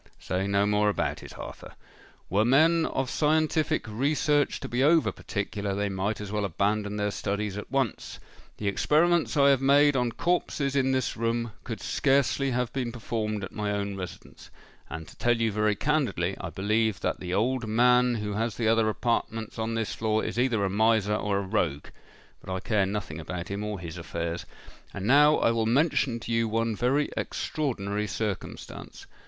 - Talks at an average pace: Yes, average, 180 wpm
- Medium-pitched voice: No, low, 110 Hz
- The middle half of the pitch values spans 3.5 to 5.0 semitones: Yes, average, 4.3 semitones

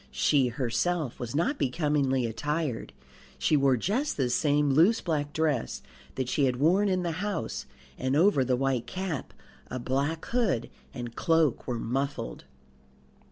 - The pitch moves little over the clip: No, average, 4.5 semitones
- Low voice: No, medium, 145 Hz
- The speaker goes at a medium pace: Yes, average, 150 wpm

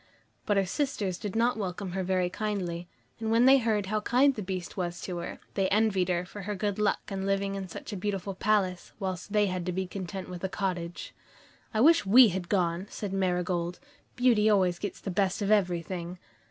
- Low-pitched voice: No, high, 195 Hz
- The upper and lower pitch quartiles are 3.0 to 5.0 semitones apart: No, narrow, 2.6 semitones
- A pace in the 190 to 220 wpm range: Yes, average, 200 wpm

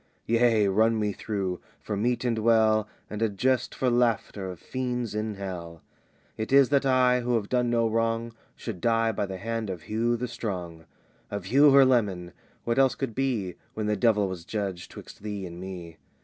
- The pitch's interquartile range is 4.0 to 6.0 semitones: No, average, 3.5 semitones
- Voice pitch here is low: Yes, low, 110 Hz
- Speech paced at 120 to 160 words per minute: No, average, 190 wpm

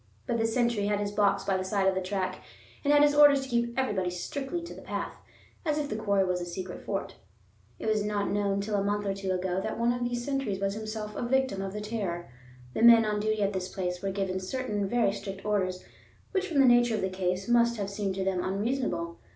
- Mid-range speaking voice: No, high, 205 Hz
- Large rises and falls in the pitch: No, average, 3.7 semitones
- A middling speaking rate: No, fast, 245 wpm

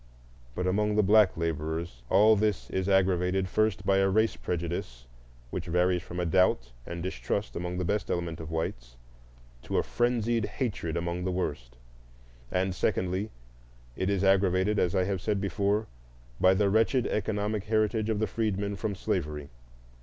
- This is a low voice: Yes, very low, 95 Hz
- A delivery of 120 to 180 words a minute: Yes, average, 160 wpm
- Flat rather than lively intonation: No, average, 3.2 semitones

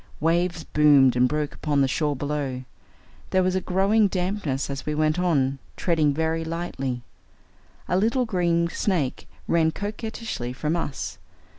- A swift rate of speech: No, average, 145 wpm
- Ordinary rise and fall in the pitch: Yes, average, 4.4 semitones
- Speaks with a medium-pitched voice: Yes, medium, 160 Hz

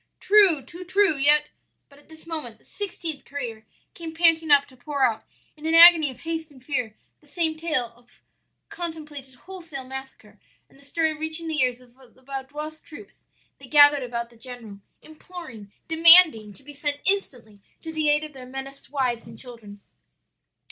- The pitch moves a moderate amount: Yes, average, 4.2 semitones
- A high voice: Yes, very high, 290 Hz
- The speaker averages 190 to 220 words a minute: No, average, 180 wpm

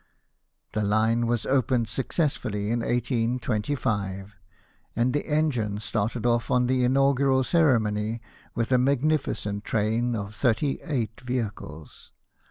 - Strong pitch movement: No, average, 3.5 semitones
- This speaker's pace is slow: Yes, slow, 115 wpm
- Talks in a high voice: No, low, 120 Hz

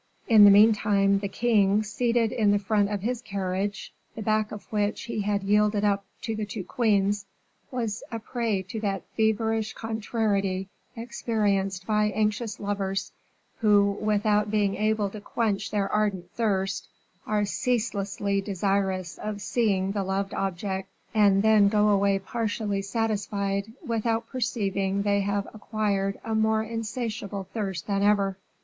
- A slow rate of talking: No, average, 145 wpm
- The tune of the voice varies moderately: No, narrow, 1.8 semitones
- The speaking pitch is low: No, high, 205 Hz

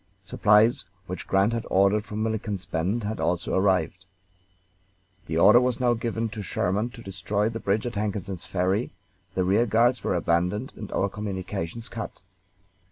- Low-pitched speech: Yes, low, 105 Hz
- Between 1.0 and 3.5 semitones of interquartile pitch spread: Yes, average, 3.2 semitones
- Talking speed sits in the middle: Yes, average, 160 wpm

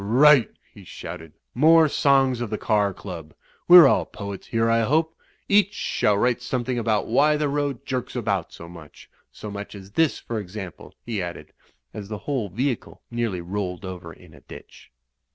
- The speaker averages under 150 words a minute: No, average, 180 wpm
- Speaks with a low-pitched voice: Yes, low, 115 Hz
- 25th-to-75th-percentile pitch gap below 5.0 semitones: No, wide, 5.5 semitones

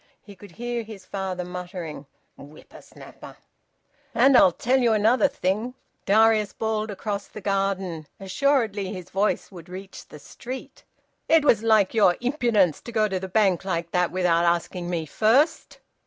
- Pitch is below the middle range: No, high, 200 Hz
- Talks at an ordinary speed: Yes, average, 155 wpm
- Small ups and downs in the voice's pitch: No, average, 3.8 semitones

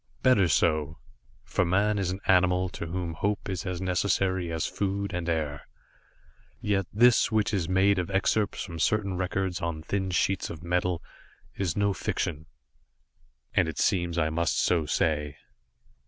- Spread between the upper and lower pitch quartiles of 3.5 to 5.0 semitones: No, average, 2.8 semitones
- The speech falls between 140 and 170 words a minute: Yes, average, 155 wpm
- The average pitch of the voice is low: Yes, very low, 90 Hz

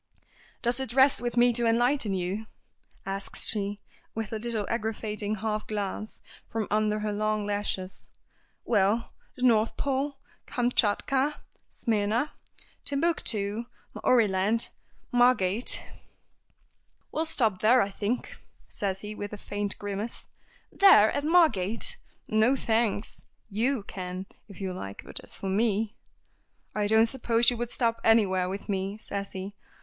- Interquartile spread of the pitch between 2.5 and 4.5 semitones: Yes, average, 2.9 semitones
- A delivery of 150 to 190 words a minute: No, slow, 135 wpm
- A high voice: Yes, high, 215 Hz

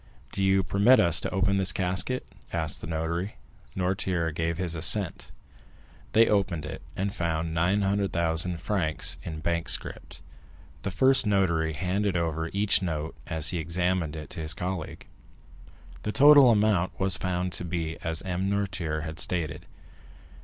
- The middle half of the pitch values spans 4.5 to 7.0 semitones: No, average, 3.1 semitones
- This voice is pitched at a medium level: No, very low, 90 Hz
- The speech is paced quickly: No, average, 150 wpm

